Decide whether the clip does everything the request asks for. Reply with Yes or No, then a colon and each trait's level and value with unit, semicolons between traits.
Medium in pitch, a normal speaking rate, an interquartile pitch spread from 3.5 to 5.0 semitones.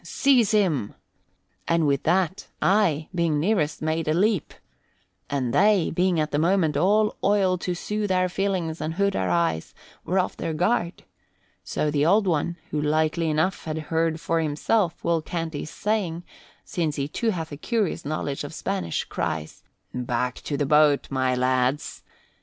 Yes: medium, 165 Hz; average, 165 wpm; average, 4.2 semitones